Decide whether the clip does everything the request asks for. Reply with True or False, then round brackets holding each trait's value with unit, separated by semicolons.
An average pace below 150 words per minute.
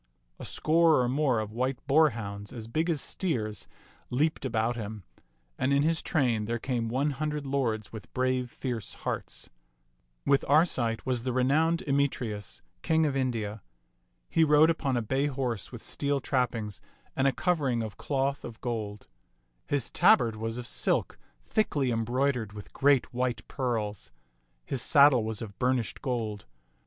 False (155 wpm)